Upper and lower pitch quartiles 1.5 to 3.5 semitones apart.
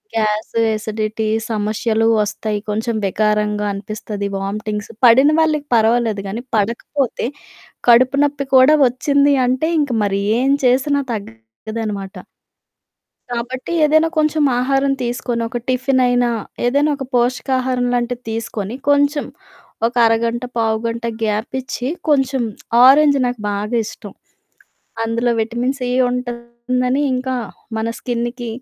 Yes: average, 3.1 semitones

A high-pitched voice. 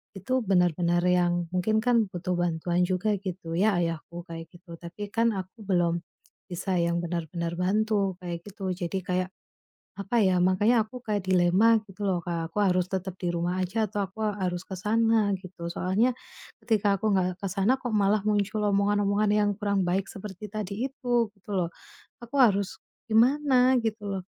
Yes: high, 195 Hz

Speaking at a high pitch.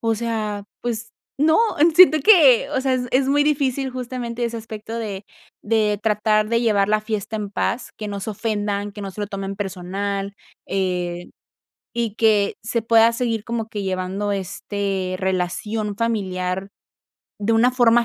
Yes: high, 215 Hz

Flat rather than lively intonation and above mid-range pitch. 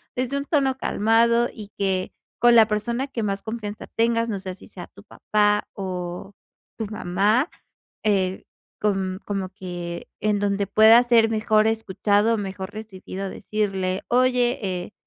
No: average, 3.0 semitones; high, 210 Hz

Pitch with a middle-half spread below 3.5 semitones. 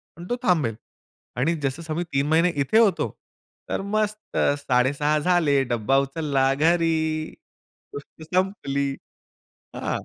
No: average, 4.1 semitones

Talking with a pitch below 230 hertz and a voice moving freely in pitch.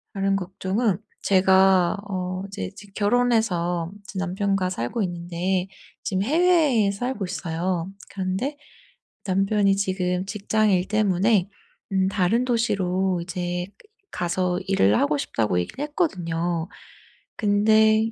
No: high, 190 Hz; average, 2.9 semitones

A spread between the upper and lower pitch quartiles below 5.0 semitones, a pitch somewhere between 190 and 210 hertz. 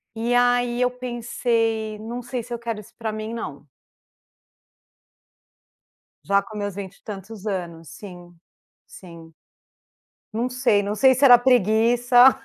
No: average, 3.3 semitones; high, 225 Hz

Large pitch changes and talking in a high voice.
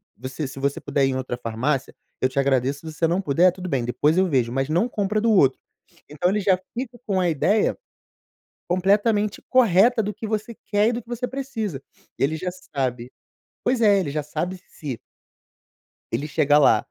No: wide, 7.3 semitones; medium, 175 Hz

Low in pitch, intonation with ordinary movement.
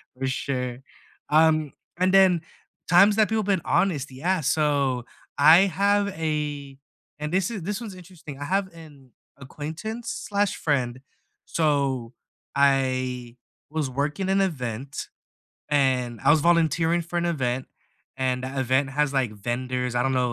No: medium, 145 Hz; average, 5.0 semitones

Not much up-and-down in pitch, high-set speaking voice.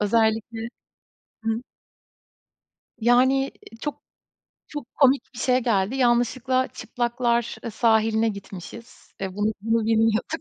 Yes: narrow, 2.2 semitones; high, 230 Hz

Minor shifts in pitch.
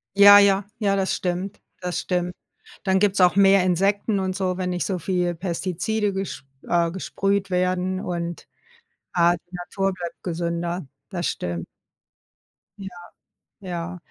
Yes: narrow, 1.8 semitones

